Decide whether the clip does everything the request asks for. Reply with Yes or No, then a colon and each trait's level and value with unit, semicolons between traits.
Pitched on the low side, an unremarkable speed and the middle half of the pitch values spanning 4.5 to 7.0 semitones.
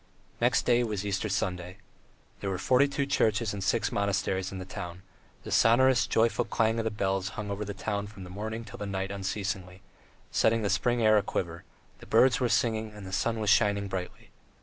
No: low, 100 Hz; average, 190 wpm; average, 2.8 semitones